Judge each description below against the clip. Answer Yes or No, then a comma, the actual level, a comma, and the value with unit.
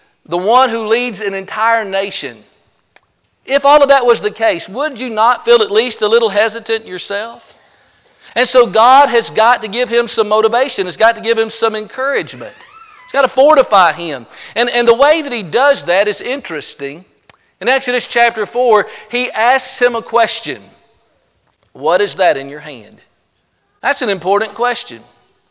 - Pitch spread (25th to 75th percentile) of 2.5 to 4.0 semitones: Yes, average, 3.7 semitones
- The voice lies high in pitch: Yes, high, 230 Hz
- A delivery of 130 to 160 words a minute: No, average, 175 wpm